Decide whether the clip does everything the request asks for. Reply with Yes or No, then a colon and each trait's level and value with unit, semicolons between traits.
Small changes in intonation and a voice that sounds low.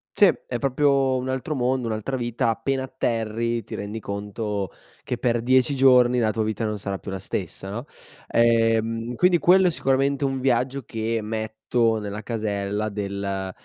No: average, 3.5 semitones; low, 115 Hz